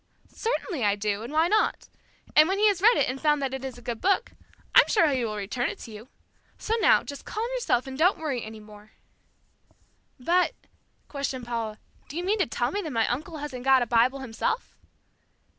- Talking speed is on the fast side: Yes, fast, 210 wpm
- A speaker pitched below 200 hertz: No, very high, 265 Hz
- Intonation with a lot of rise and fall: Yes, wide, 6.7 semitones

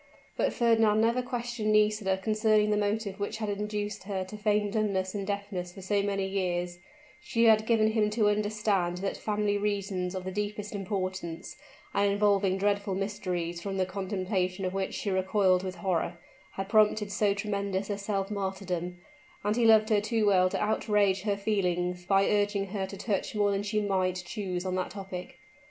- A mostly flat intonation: Yes, narrow, 1.9 semitones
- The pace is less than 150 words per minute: No, average, 180 wpm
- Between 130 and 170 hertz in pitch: No, high, 200 Hz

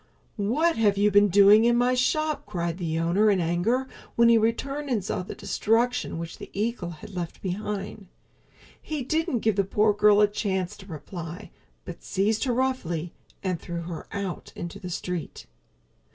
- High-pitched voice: Yes, high, 205 Hz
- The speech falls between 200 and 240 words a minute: No, average, 175 wpm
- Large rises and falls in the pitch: No, average, 4.8 semitones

